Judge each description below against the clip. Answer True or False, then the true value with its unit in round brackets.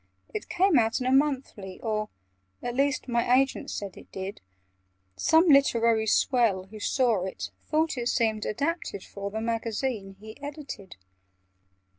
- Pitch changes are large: False (4.5 semitones)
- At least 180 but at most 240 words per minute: False (145 wpm)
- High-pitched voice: True (235 Hz)